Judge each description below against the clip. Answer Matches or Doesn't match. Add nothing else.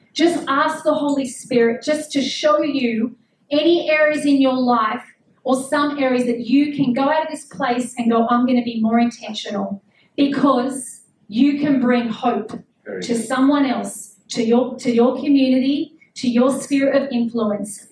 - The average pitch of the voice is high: Matches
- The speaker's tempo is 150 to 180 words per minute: Matches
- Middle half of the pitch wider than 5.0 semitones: Doesn't match